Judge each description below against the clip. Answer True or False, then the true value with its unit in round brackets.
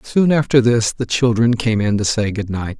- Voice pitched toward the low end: True (115 Hz)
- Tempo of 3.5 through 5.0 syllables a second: True (4.8 syllables/s)